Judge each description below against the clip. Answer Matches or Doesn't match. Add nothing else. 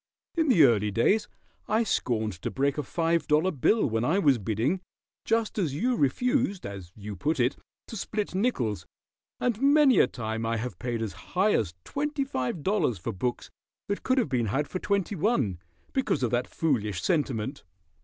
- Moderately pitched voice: Matches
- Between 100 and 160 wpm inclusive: Doesn't match